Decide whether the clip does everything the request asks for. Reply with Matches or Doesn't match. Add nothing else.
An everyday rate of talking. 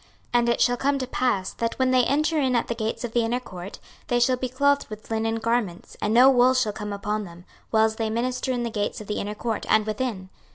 Doesn't match